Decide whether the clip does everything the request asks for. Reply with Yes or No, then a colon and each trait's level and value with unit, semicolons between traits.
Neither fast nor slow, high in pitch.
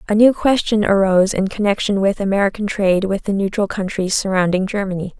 Yes: average, 175 wpm; high, 200 Hz